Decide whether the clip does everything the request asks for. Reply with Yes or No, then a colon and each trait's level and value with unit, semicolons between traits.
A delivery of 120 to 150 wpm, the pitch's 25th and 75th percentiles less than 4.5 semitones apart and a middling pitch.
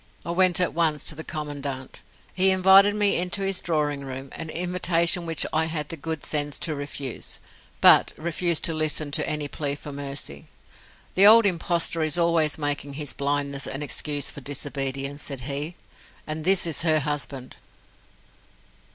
No: average, 165 wpm; average, 3.2 semitones; medium, 155 Hz